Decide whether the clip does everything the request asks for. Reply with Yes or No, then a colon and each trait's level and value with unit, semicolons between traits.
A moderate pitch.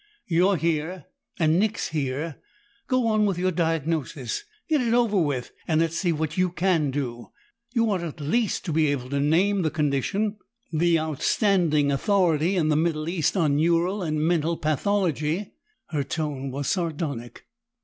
Yes: medium, 165 Hz